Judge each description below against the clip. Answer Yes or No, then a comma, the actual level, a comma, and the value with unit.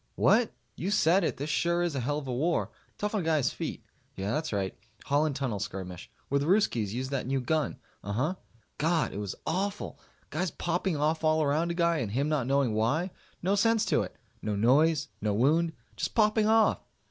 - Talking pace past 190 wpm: Yes, fast, 205 wpm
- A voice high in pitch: No, medium, 150 Hz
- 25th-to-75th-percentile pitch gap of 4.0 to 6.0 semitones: Yes, wide, 5.5 semitones